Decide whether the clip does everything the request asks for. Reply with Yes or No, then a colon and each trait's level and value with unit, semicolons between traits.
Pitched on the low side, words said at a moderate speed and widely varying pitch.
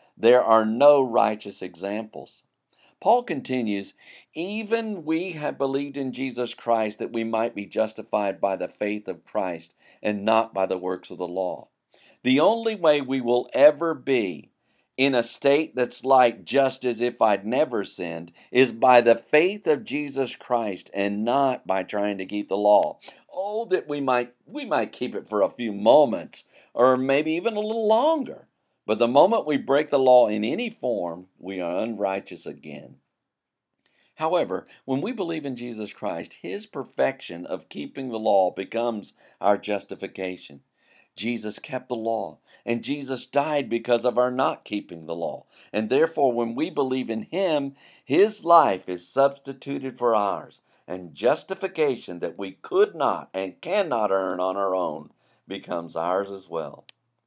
Yes: low, 120 Hz; average, 165 wpm; wide, 5.8 semitones